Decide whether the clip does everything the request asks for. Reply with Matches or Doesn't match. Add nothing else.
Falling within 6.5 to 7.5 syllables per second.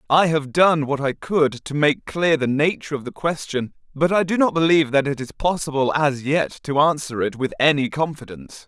Doesn't match